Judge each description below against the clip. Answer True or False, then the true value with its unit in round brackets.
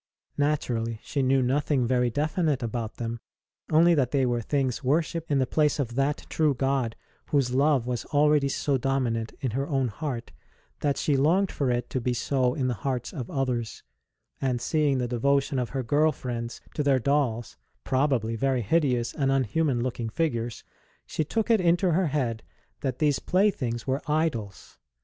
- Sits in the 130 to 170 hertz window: True (135 Hz)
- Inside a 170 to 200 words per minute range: True (175 wpm)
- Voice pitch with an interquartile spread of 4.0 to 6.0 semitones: False (3.4 semitones)